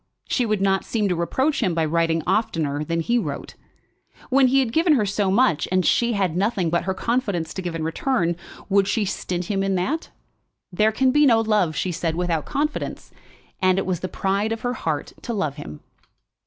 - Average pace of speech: No, fast, 210 wpm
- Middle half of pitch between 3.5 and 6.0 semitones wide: Yes, average, 5.2 semitones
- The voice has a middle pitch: No, high, 195 Hz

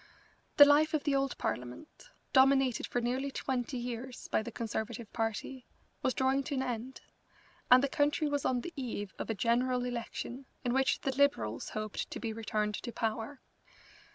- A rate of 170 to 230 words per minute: Yes, average, 175 wpm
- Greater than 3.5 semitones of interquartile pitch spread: No, average, 3.0 semitones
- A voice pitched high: Yes, very high, 250 Hz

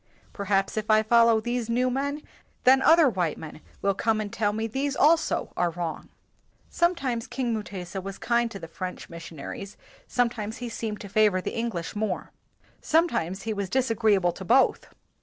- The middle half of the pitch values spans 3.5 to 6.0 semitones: Yes, average, 4.2 semitones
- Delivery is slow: No, average, 175 wpm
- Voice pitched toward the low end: No, high, 220 Hz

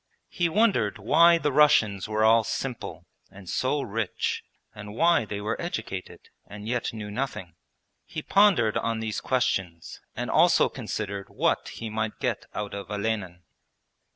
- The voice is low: Yes, low, 110 Hz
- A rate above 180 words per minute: No, average, 150 wpm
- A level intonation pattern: No, average, 4.6 semitones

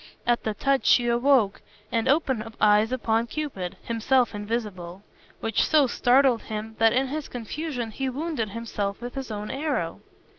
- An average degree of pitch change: Yes, average, 3.8 semitones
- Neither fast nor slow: Yes, average, 155 wpm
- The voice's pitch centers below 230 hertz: No, high, 235 Hz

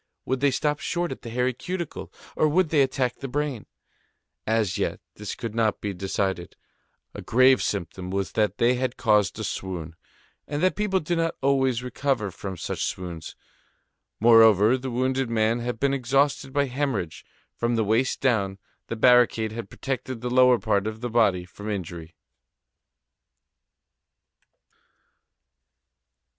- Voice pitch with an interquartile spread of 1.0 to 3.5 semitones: No, average, 4.3 semitones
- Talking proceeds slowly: No, average, 150 wpm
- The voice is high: No, low, 120 Hz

